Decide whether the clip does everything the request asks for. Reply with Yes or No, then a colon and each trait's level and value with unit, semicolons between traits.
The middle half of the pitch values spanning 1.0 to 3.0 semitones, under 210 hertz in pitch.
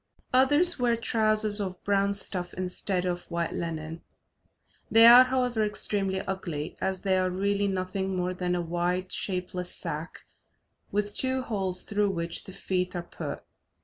Yes: average, 2.7 semitones; high, 190 Hz